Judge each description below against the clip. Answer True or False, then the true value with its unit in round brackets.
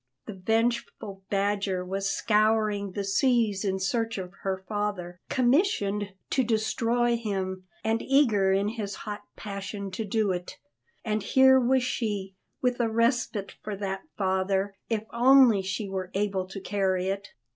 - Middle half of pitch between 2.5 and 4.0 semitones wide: True (2.9 semitones)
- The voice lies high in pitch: True (205 Hz)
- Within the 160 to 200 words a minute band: False (145 wpm)